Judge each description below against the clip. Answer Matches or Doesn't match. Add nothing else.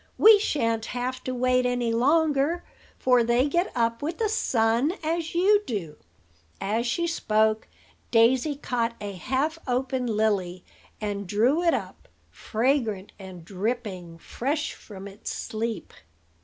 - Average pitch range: Matches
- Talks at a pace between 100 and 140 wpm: Matches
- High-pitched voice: Matches